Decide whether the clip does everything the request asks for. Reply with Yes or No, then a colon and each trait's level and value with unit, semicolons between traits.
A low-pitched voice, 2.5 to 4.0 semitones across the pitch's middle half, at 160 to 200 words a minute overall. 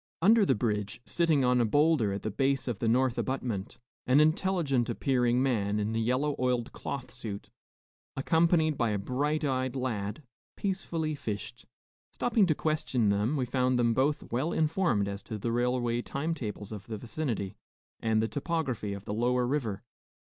No: low, 125 Hz; average, 5.0 semitones; average, 170 wpm